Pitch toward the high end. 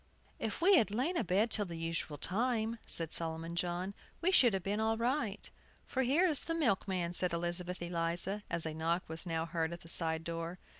No: medium, 180 Hz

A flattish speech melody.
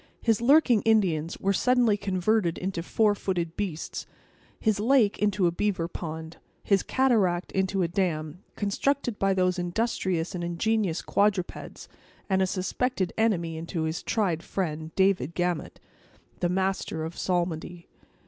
No: average, 3.5 semitones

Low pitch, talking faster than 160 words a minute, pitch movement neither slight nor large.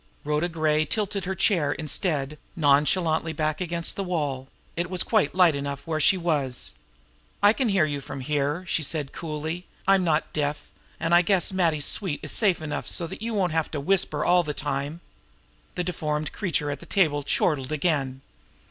No: medium, 160 Hz; average, 185 wpm; average, 3.4 semitones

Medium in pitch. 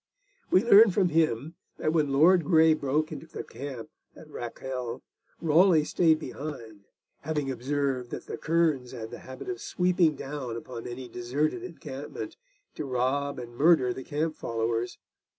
Yes: medium, 145 Hz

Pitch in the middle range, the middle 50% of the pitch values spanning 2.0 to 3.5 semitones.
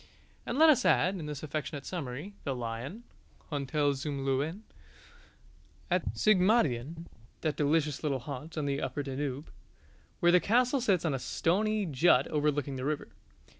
No: medium, 150 Hz; average, 4.6 semitones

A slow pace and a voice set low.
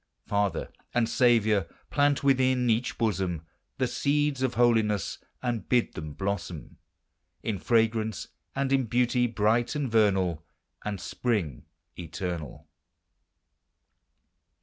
Yes: slow, 105 wpm; low, 115 Hz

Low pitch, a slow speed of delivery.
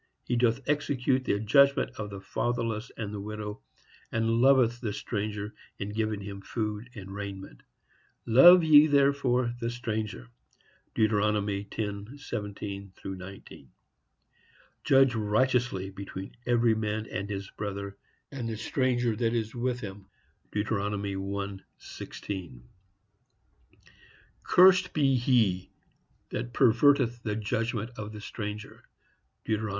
Yes: low, 110 Hz; slow, 105 wpm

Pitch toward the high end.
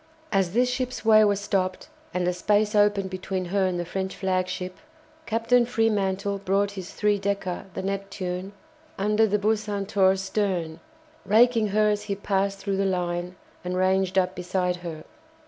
Yes: high, 195 Hz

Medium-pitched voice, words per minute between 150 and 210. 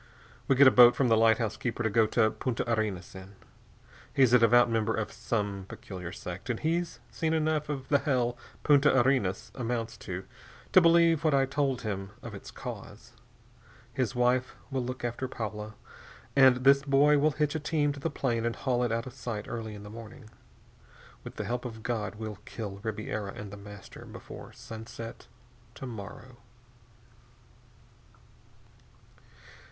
No: low, 120 Hz; average, 170 wpm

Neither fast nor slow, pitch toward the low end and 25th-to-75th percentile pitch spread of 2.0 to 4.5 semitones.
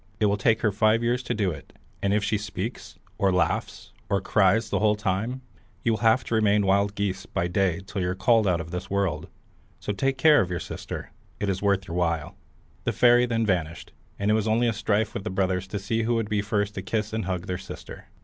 No: fast, 240 wpm; low, 100 Hz; average, 2.8 semitones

